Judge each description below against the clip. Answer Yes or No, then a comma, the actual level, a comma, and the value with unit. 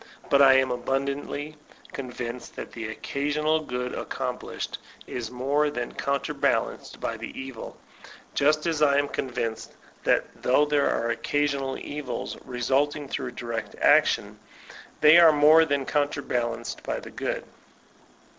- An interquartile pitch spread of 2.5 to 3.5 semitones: Yes, average, 2.9 semitones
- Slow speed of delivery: Yes, slow, 130 wpm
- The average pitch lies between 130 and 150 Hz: Yes, medium, 140 Hz